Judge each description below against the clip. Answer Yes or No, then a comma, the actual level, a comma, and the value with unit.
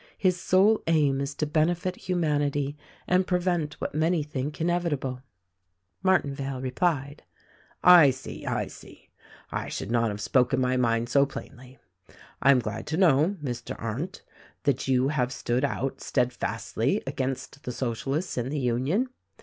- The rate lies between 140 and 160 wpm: Yes, average, 150 wpm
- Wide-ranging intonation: No, average, 4.4 semitones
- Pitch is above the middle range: No, medium, 140 Hz